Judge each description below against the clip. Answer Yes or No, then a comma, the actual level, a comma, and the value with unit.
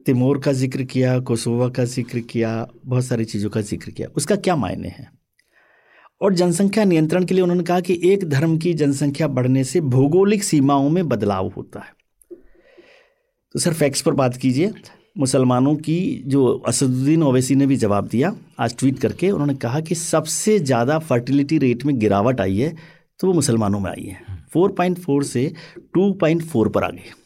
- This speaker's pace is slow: No, average, 175 wpm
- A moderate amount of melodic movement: No, wide, 5.8 semitones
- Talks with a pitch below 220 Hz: Yes, medium, 140 Hz